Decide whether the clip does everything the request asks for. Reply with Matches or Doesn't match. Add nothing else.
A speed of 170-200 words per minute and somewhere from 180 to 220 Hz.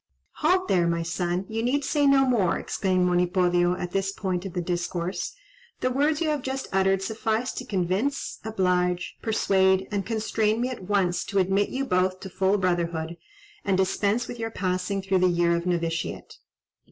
Matches